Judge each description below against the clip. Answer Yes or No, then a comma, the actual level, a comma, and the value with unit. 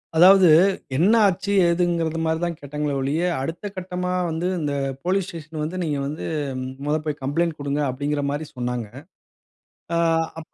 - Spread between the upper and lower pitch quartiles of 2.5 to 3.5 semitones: Yes, average, 3.0 semitones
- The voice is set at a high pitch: No, medium, 160 Hz